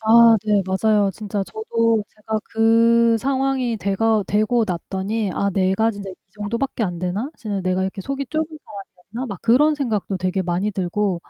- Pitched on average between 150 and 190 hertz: No, high, 215 Hz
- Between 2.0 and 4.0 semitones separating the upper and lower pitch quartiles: Yes, average, 3.2 semitones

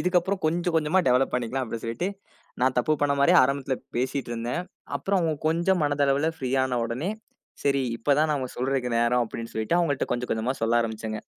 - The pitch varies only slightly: No, average, 4.7 semitones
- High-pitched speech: No, low, 135 Hz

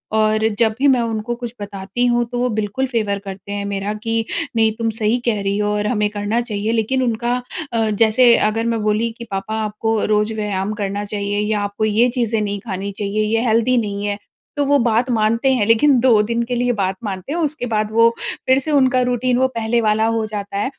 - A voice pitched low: No, high, 220 Hz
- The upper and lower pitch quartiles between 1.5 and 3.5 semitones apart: Yes, narrow, 2.5 semitones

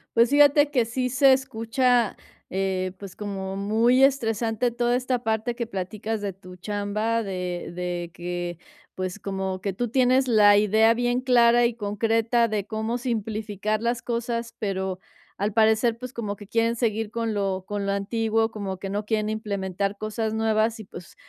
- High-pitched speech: Yes, high, 220 Hz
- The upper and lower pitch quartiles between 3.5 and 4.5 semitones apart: No, average, 2.9 semitones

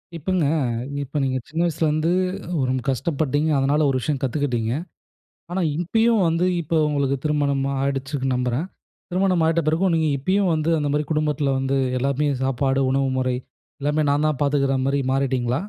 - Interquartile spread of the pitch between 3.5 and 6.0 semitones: No, average, 2.9 semitones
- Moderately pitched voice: Yes, medium, 145 Hz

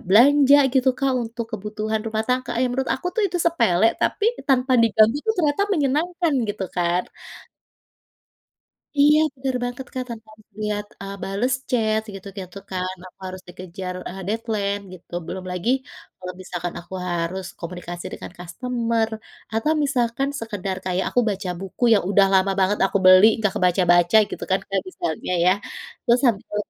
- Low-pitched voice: No, high, 210 Hz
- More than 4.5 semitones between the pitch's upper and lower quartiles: Yes, average, 5.2 semitones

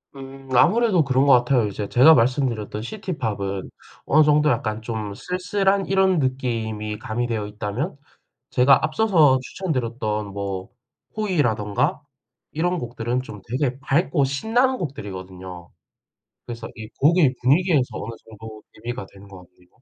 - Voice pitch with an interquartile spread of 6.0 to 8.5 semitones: Yes, wide, 6.3 semitones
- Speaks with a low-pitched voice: Yes, low, 125 Hz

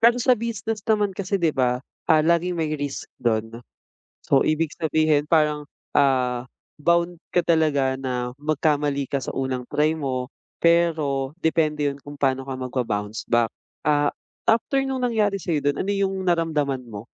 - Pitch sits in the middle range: Yes, medium, 150 Hz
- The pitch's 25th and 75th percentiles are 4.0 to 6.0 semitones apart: Yes, average, 4.3 semitones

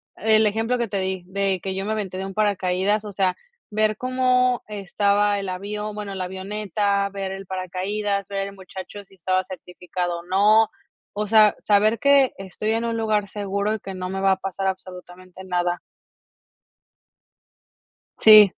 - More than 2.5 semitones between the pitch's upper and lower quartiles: No, narrow, 2.1 semitones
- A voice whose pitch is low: No, high, 200 Hz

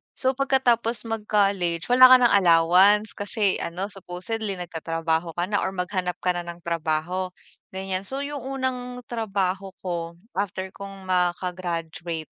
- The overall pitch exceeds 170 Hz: Yes, high, 190 Hz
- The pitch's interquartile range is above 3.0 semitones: Yes, average, 4.0 semitones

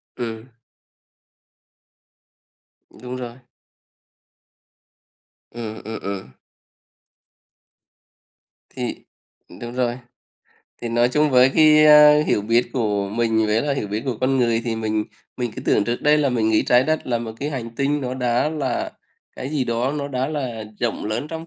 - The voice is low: Yes, low, 120 Hz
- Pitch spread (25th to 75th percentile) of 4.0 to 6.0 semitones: No, average, 3.5 semitones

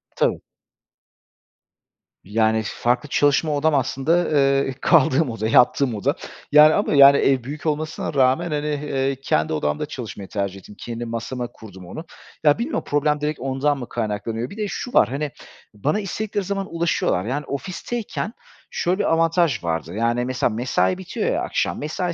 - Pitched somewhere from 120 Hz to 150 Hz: Yes, medium, 140 Hz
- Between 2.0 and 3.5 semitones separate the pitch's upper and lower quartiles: No, average, 5.2 semitones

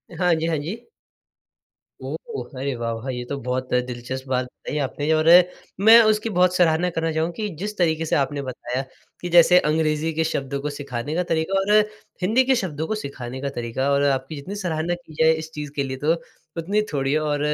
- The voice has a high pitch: No, medium, 155 Hz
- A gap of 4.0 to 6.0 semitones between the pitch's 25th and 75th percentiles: Yes, average, 4.4 semitones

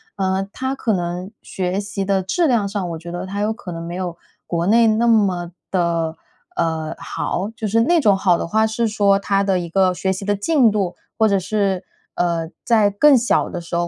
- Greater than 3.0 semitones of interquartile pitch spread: Yes, average, 3.6 semitones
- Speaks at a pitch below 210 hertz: Yes, high, 195 Hz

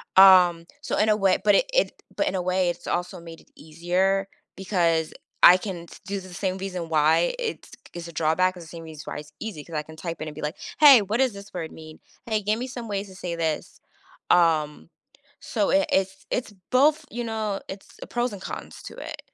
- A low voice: No, medium, 185 Hz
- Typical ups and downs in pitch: Yes, average, 4.0 semitones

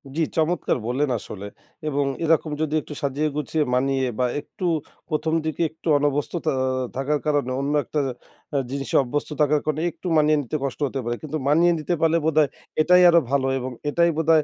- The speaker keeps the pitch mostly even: Yes, narrow, 2.3 semitones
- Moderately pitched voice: Yes, medium, 150 Hz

